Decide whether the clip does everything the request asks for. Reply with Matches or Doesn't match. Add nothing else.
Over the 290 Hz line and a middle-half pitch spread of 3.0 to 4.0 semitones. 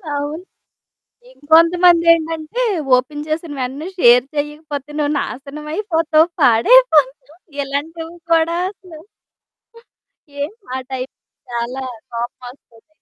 Matches